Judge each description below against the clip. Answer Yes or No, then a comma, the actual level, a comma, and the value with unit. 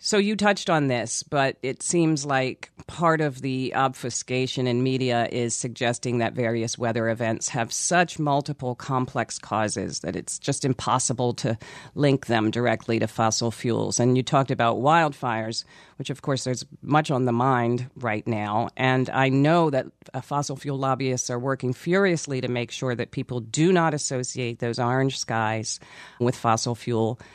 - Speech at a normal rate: Yes, average, 165 wpm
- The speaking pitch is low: Yes, low, 125 Hz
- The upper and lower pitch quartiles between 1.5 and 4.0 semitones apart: Yes, average, 3.0 semitones